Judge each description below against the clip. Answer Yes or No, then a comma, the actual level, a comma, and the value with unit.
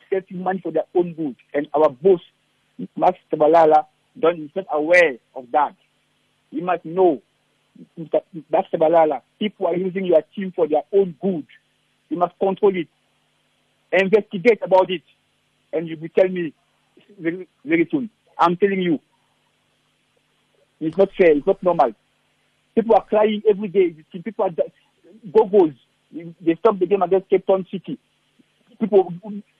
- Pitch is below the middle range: No, medium, 185 Hz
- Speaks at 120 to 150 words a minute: Yes, average, 145 wpm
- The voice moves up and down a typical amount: Yes, average, 3.6 semitones